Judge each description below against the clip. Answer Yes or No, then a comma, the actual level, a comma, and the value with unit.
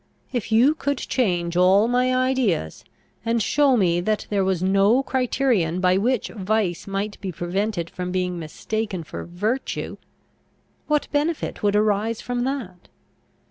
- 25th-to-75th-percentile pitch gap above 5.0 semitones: Yes, wide, 5.4 semitones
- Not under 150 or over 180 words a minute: No, average, 140 wpm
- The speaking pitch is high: Yes, high, 210 Hz